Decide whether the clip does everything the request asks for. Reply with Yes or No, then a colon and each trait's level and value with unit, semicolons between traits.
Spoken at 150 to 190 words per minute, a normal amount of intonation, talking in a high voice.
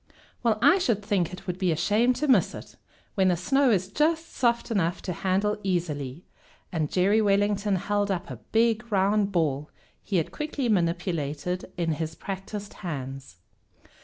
Yes: average, 165 wpm; average, 4.0 semitones; high, 195 Hz